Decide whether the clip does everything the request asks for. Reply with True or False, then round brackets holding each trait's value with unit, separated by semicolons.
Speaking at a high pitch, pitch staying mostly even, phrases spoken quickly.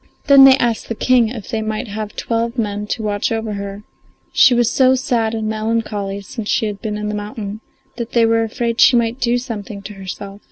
True (220 Hz; 2.1 semitones; 215 wpm)